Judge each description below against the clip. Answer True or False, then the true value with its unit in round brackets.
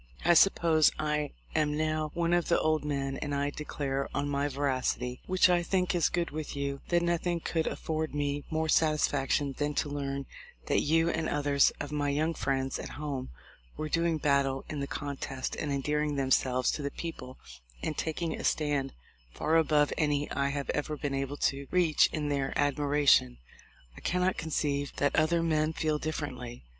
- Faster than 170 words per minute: True (180 wpm)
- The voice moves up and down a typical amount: False (2.1 semitones)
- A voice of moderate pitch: True (150 Hz)